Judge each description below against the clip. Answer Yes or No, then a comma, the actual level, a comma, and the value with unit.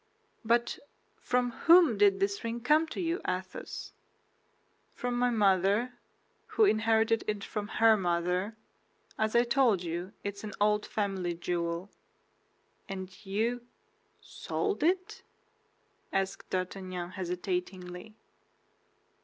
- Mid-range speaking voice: No, high, 205 Hz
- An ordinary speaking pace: No, slow, 110 wpm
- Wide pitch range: No, average, 4.3 semitones